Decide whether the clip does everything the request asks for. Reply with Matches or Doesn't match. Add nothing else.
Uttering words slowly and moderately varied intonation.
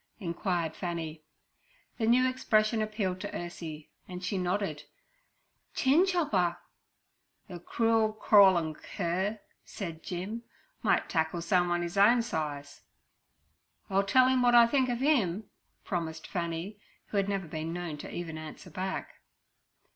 Matches